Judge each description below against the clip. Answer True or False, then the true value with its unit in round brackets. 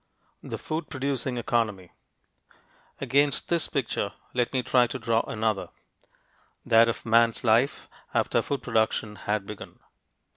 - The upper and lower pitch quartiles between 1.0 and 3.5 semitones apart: True (3.0 semitones)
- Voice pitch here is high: False (115 Hz)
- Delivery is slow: True (125 wpm)